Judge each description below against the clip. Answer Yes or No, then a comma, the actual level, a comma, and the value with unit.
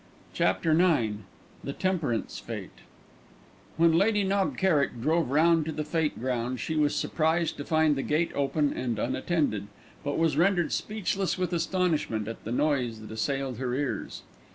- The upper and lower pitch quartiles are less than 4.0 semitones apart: No, average, 4.8 semitones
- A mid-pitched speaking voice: Yes, medium, 150 Hz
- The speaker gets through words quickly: No, average, 155 wpm